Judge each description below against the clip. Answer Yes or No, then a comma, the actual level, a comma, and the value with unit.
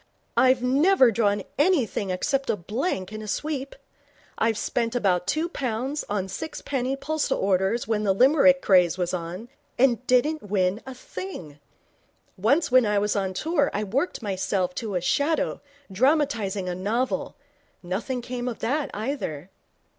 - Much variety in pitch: Yes, wide, 6.0 semitones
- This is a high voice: Yes, high, 230 Hz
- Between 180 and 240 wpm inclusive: No, average, 150 wpm